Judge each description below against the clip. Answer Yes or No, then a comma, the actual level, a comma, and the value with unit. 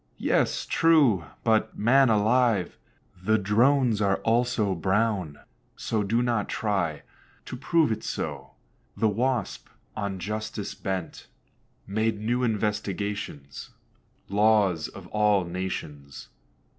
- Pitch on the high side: No, low, 105 Hz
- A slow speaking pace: Yes, slow, 105 wpm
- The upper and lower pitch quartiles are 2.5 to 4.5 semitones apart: Yes, average, 3.1 semitones